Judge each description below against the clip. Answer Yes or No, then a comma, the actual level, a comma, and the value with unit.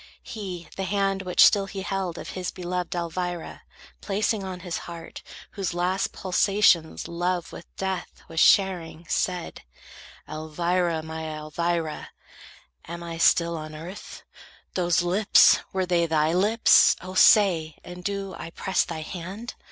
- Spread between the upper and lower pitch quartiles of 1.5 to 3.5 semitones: Yes, narrow, 2.4 semitones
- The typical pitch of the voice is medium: Yes, medium, 180 Hz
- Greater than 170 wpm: No, average, 140 wpm